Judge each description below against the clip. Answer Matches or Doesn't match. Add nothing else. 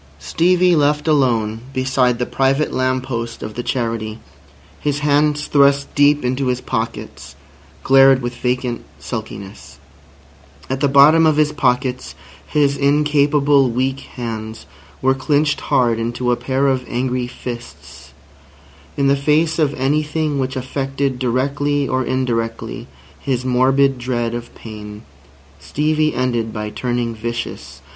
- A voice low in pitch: Matches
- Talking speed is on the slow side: Matches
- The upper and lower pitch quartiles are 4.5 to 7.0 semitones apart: Doesn't match